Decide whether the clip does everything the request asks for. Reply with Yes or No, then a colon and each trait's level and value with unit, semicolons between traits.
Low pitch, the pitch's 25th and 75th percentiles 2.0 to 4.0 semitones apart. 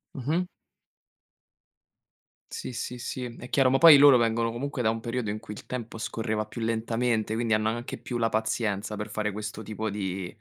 Yes: low, 115 Hz; narrow, 2.4 semitones